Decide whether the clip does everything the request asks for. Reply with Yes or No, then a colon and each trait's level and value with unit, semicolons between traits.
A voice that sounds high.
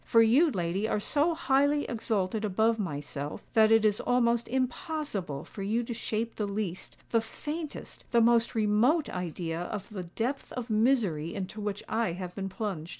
Yes: high, 220 Hz